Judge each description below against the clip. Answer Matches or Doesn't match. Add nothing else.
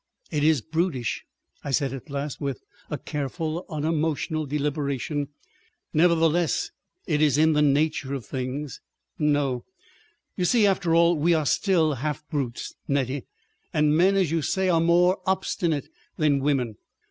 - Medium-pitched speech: Matches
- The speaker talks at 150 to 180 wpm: Doesn't match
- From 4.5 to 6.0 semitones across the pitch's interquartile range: Doesn't match